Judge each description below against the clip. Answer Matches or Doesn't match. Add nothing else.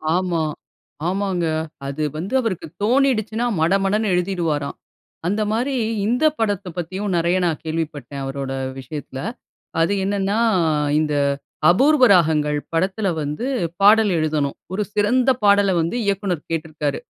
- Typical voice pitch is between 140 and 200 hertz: Matches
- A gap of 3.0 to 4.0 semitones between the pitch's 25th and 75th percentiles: Doesn't match